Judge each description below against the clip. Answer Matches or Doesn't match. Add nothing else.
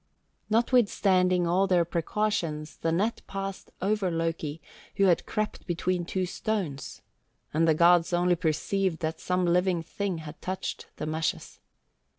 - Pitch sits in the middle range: Matches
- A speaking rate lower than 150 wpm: Matches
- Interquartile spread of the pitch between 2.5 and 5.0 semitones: Matches